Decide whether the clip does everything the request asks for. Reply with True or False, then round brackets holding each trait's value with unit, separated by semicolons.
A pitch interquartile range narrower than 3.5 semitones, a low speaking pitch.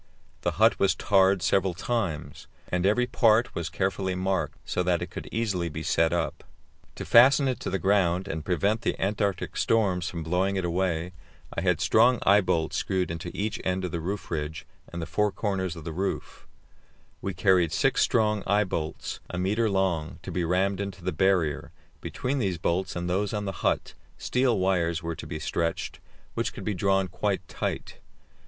True (3.0 semitones; 95 Hz)